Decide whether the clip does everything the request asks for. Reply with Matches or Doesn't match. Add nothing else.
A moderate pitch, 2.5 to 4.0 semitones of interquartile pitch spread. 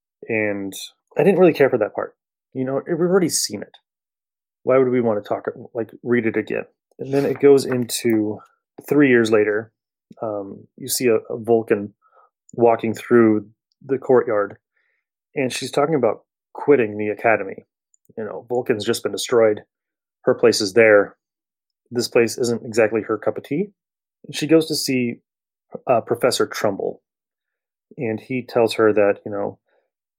Doesn't match